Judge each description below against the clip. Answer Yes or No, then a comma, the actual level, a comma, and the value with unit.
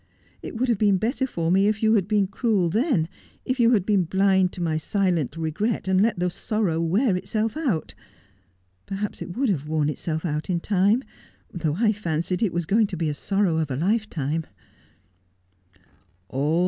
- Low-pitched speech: No, high, 190 Hz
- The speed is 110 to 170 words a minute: No, average, 185 wpm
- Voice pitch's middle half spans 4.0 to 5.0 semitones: Yes, average, 4.7 semitones